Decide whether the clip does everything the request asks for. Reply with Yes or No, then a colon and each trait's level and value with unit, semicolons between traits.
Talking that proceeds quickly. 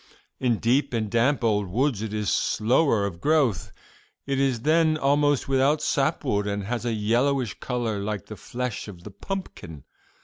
No: average, 170 wpm